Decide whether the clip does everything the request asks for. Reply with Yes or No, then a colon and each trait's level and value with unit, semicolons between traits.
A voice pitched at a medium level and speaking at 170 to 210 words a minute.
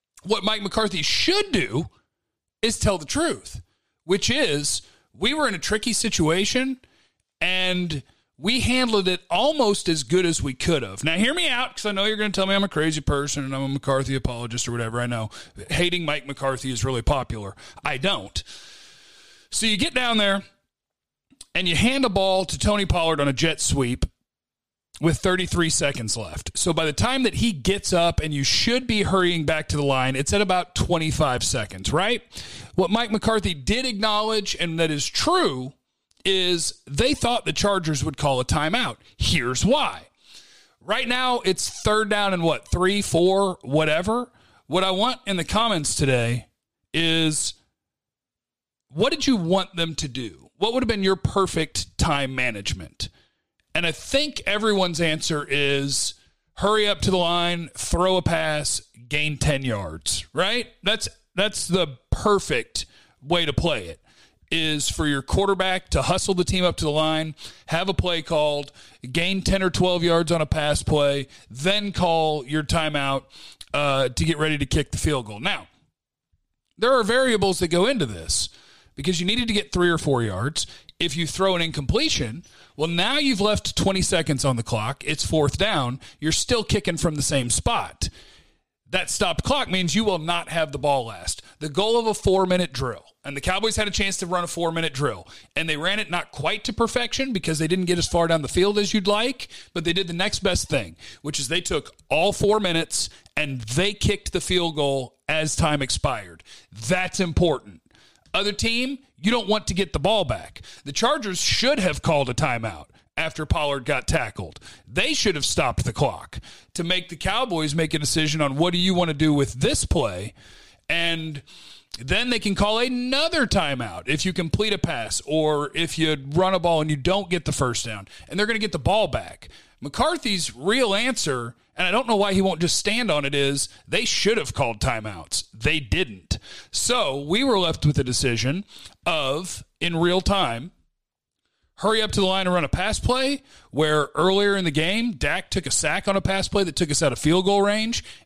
Yes: medium, 170 Hz; average, 195 wpm